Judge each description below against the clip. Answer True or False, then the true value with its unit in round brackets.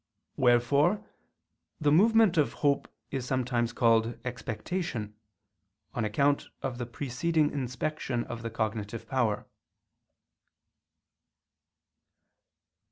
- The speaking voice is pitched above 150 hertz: False (125 Hz)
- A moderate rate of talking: False (90 wpm)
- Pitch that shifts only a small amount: False (4.0 semitones)